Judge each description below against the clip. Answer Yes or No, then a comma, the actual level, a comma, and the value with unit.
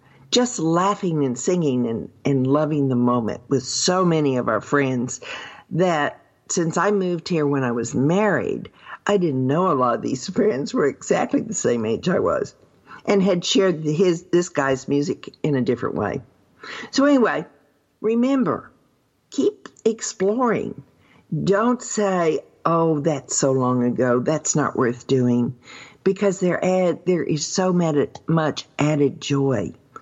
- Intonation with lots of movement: Yes, wide, 5.9 semitones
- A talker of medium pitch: Yes, medium, 160 Hz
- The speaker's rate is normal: Yes, average, 145 wpm